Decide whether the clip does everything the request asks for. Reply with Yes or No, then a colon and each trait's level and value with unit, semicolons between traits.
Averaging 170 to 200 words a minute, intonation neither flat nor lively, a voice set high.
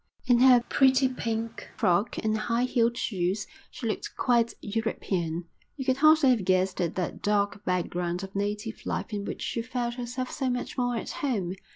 Yes: average, 180 wpm; average, 4.2 semitones; high, 230 Hz